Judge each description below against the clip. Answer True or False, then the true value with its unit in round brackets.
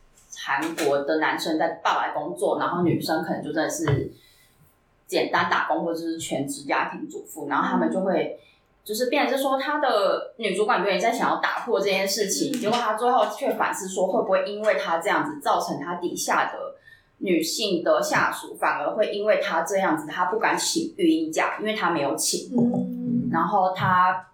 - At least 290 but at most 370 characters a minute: False (280 characters per minute)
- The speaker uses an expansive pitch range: True (8.1 semitones)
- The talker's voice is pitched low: False (195 Hz)